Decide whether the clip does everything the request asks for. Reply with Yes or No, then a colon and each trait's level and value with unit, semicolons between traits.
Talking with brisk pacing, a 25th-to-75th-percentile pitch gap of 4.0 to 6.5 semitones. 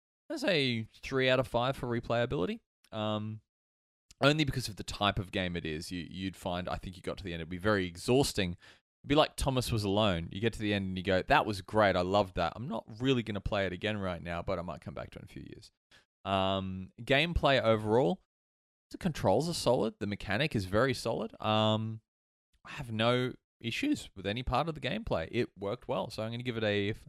Yes: fast, 235 wpm; average, 4.5 semitones